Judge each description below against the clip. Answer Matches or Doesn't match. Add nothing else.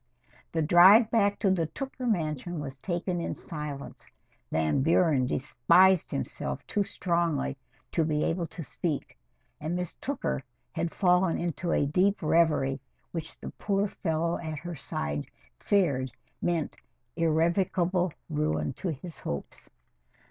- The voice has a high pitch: Doesn't match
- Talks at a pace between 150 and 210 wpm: Doesn't match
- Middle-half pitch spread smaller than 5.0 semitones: Matches